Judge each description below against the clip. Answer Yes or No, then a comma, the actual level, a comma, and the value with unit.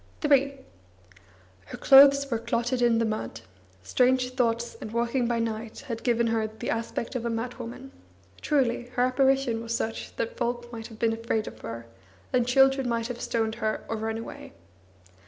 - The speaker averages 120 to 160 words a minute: No, average, 175 wpm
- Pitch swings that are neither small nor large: No, narrow, 1.9 semitones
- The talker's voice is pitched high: Yes, high, 235 Hz